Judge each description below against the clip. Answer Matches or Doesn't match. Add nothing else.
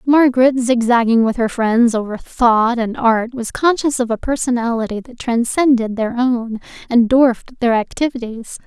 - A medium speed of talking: Matches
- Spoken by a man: Doesn't match